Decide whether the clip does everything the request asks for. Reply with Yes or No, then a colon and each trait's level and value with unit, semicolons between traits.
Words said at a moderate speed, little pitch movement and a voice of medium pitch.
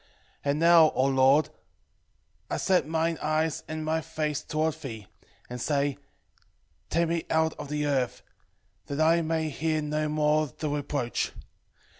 Yes: average, 160 wpm; narrow, 1.9 semitones; medium, 155 Hz